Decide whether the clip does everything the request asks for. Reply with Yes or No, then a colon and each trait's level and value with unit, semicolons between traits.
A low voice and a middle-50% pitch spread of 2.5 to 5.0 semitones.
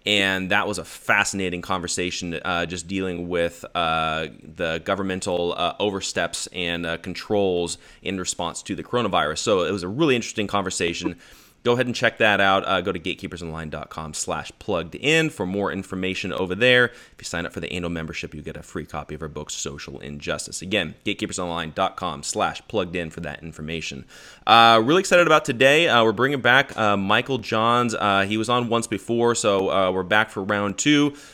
Yes: very low, 95 Hz; average, 4.7 semitones